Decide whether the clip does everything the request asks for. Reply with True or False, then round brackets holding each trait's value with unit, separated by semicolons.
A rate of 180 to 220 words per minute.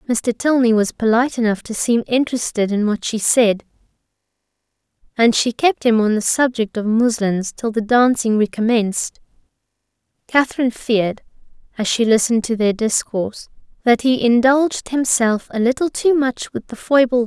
False (160 wpm)